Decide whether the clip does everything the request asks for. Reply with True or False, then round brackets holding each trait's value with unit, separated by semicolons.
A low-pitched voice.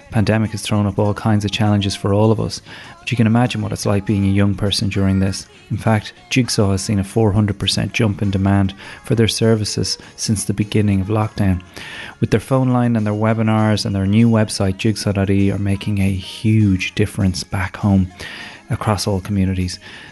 True (105 Hz)